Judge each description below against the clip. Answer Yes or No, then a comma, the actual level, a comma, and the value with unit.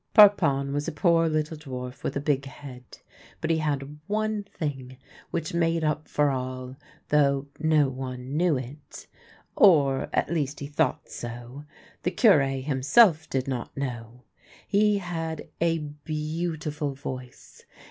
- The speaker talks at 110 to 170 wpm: Yes, average, 145 wpm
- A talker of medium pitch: Yes, medium, 145 Hz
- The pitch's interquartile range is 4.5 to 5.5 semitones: No, average, 3.4 semitones